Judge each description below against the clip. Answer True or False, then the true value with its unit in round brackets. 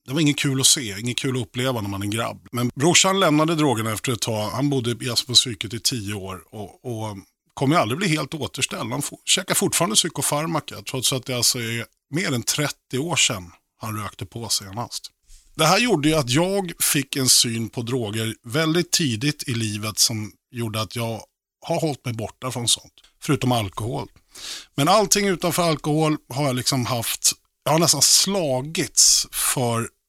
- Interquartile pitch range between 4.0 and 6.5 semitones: True (5.0 semitones)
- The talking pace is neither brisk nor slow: True (185 wpm)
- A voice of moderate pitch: False (125 Hz)